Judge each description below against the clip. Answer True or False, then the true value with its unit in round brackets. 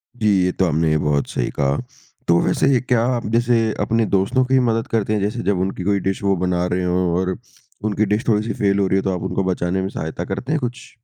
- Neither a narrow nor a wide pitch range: True (3.9 semitones)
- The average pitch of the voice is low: True (95 Hz)